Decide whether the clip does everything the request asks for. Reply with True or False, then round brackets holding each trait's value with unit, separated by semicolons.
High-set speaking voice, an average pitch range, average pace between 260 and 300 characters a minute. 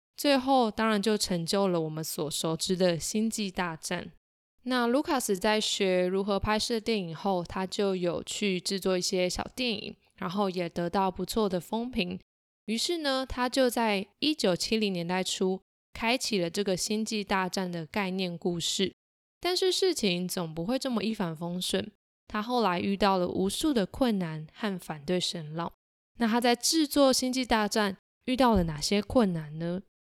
False (200 Hz; 4.1 semitones; 250 characters per minute)